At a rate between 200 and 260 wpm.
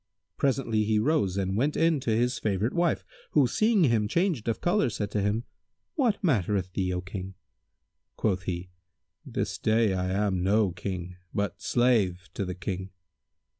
No: average, 165 wpm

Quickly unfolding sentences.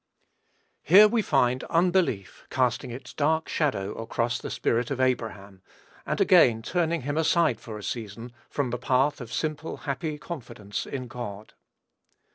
No: average, 145 wpm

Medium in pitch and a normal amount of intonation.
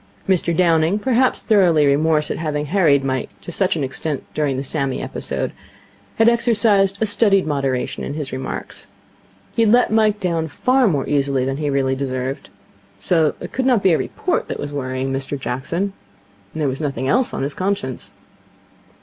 No: medium, 155 Hz; wide, 6.4 semitones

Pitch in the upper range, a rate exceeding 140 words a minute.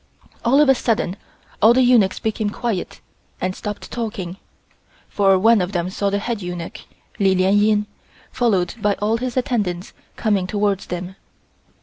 Yes: high, 205 Hz; average, 155 wpm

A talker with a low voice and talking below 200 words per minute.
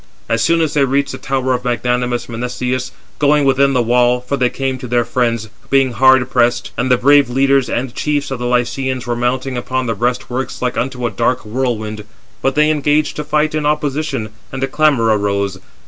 No: low, 125 Hz; fast, 205 wpm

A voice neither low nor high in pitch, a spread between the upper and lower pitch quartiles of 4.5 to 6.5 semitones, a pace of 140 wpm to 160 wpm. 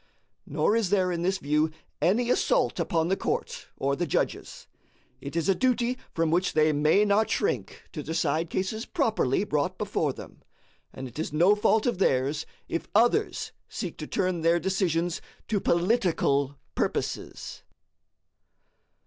Yes: medium, 175 Hz; average, 5.0 semitones; average, 150 wpm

